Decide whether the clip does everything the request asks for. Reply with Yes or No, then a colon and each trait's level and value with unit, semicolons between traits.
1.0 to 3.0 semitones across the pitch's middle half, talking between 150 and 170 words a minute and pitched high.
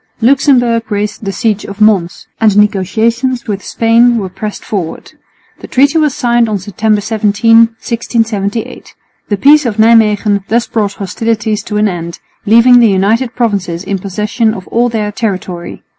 Yes: narrow, 2.6 semitones; average, 160 wpm; high, 215 Hz